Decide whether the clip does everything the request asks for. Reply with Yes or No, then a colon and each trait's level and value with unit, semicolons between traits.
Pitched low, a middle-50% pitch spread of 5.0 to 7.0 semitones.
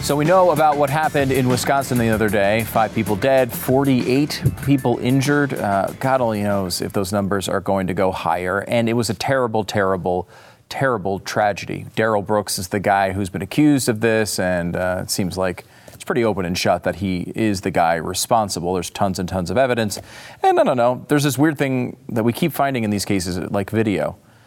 Yes: low, 110 Hz; wide, 5.4 semitones